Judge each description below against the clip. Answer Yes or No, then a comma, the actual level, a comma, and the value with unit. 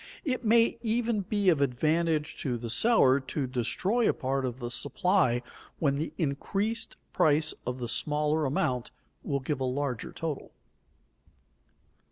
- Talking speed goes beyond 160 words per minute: No, average, 145 wpm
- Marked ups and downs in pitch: Yes, wide, 6.6 semitones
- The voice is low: No, medium, 150 Hz